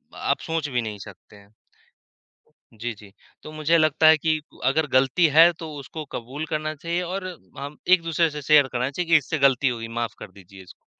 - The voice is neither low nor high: Yes, medium, 145 Hz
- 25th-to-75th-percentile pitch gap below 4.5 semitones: No, average, 5.0 semitones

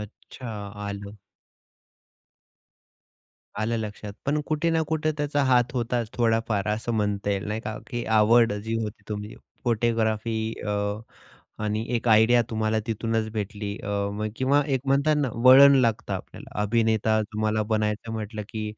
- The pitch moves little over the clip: Yes, narrow, 2.1 semitones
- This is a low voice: Yes, low, 110 Hz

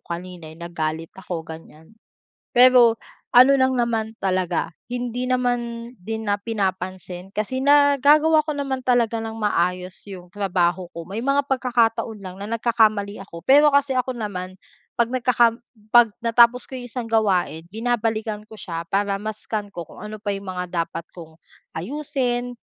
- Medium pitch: No, high, 220 Hz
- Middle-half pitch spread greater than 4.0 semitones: Yes, average, 5.0 semitones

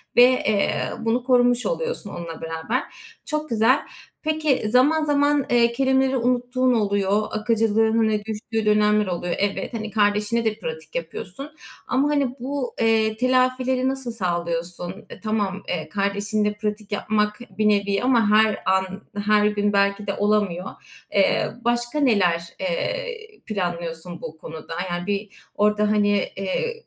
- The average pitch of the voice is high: Yes, high, 215 Hz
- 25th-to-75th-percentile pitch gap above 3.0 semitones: Yes, average, 3.9 semitones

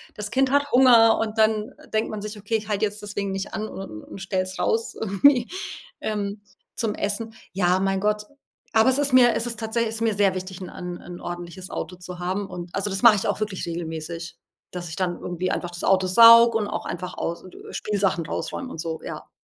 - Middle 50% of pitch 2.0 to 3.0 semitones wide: No, average, 3.4 semitones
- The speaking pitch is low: No, high, 200 Hz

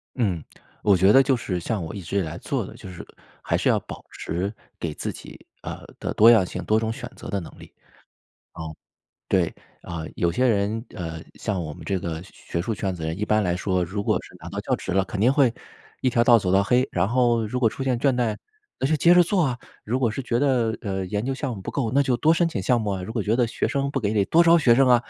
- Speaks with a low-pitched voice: Yes, low, 110 Hz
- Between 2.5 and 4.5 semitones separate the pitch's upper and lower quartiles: No, average, 5.1 semitones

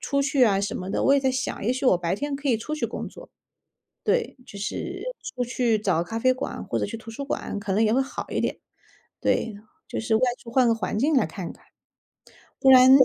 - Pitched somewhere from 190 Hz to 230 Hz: No, high, 245 Hz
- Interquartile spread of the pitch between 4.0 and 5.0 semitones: Yes, average, 4.3 semitones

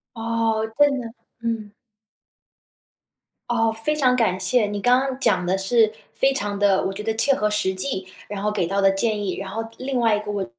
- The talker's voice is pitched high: Yes, high, 215 Hz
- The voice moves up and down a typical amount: Yes, average, 3.2 semitones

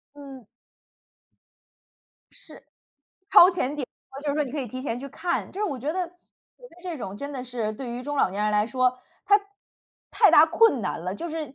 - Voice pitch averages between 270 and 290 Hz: Yes, very high, 275 Hz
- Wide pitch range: No, average, 4.5 semitones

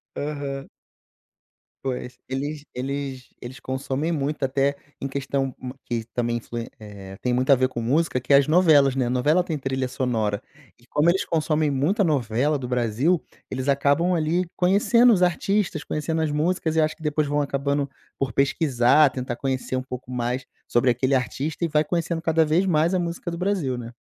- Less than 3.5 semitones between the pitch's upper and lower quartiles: No, average, 3.8 semitones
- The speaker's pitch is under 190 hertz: Yes, medium, 140 Hz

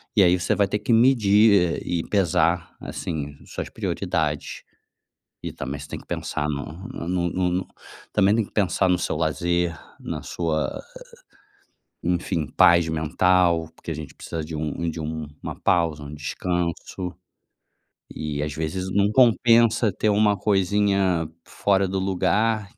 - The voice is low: Yes, very low, 90 Hz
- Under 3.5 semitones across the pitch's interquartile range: No, average, 3.8 semitones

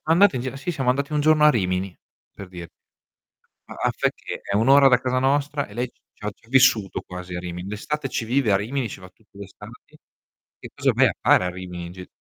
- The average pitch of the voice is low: Yes, low, 115 Hz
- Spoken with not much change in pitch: No, wide, 6.9 semitones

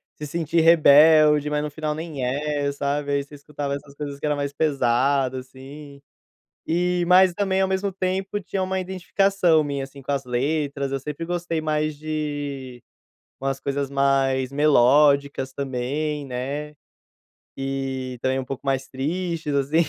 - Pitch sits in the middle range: Yes, medium, 145 Hz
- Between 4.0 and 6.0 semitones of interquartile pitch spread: No, narrow, 2.6 semitones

